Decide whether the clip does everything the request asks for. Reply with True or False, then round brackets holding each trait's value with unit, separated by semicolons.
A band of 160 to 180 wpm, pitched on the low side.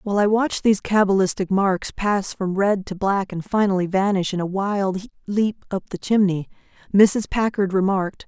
False (175 wpm; 195 Hz)